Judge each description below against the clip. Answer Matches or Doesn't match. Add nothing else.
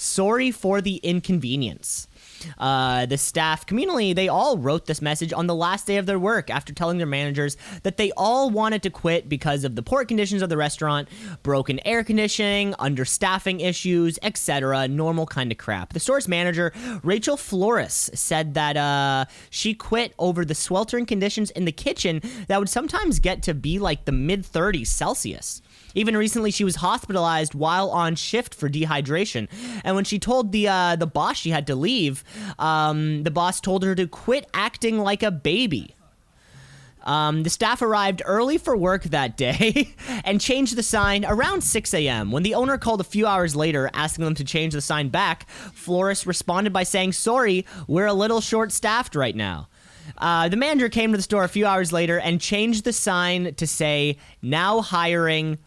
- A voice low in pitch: Doesn't match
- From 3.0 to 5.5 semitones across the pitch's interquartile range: Matches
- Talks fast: Doesn't match